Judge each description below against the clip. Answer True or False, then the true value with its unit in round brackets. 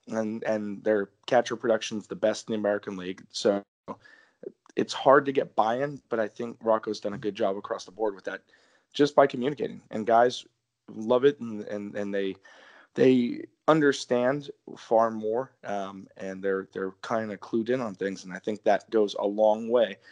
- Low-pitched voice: True (110 Hz)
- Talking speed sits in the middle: True (190 wpm)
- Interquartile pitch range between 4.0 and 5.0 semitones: False (2.7 semitones)